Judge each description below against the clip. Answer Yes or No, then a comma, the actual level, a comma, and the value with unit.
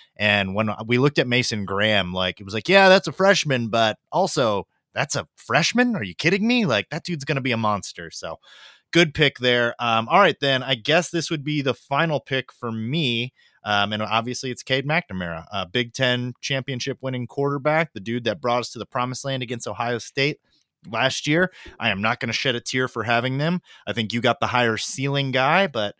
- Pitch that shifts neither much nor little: Yes, average, 4.6 semitones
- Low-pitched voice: Yes, low, 125 Hz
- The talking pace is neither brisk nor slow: No, fast, 220 wpm